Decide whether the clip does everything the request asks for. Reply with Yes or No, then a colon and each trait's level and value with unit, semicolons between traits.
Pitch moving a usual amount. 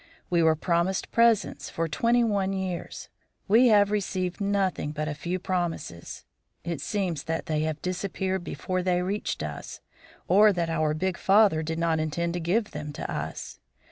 Yes: average, 3.5 semitones